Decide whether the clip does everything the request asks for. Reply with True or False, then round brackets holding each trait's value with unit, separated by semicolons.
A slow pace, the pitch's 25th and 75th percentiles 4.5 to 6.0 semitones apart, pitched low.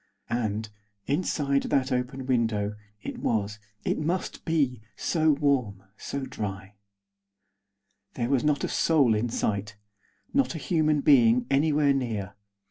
True (130 wpm; 5.2 semitones; 130 Hz)